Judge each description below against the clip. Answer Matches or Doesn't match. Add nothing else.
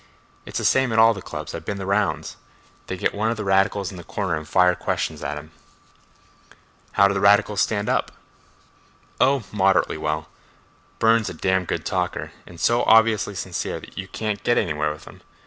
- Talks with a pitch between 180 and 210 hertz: Doesn't match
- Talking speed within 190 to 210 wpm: Matches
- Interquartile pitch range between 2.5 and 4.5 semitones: Matches